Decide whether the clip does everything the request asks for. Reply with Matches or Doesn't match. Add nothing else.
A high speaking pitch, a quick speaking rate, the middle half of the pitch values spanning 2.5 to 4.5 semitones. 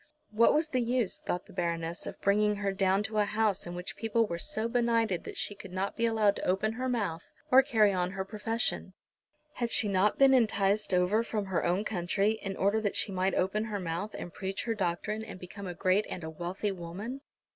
Matches